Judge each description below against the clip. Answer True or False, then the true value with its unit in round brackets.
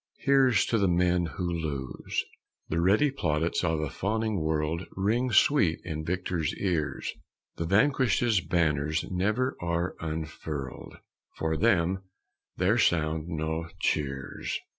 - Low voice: True (85 Hz)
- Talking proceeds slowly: True (120 wpm)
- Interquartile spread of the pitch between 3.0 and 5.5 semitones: True (4.3 semitones)